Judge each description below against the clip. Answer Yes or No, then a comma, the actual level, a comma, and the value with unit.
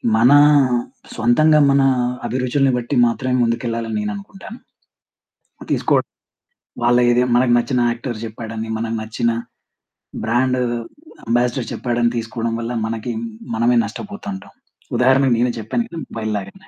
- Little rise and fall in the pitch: Yes, narrow, 2.2 semitones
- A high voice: No, low, 120 Hz